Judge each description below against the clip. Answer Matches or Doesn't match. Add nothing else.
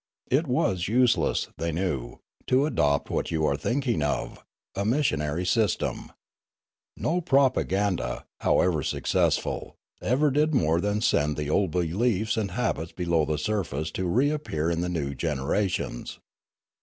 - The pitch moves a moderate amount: Doesn't match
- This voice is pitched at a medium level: Doesn't match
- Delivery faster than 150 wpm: Doesn't match